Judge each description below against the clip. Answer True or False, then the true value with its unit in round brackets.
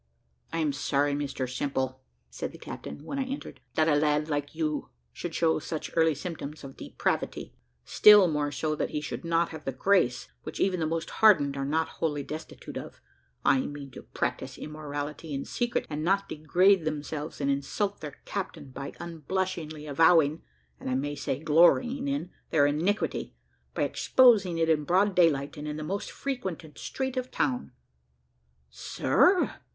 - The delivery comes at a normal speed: True (170 wpm)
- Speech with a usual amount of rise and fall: True (3.7 semitones)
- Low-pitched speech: False (155 Hz)